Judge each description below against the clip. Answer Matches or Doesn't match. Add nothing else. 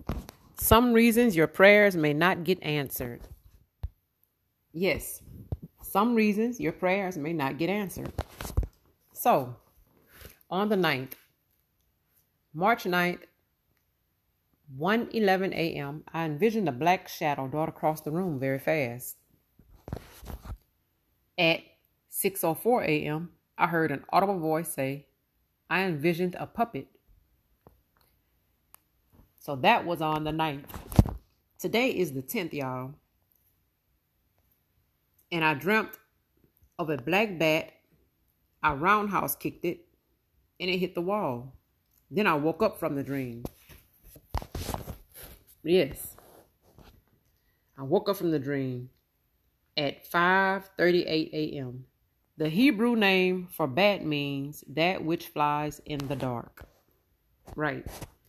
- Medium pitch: Matches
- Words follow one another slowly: Matches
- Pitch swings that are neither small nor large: Doesn't match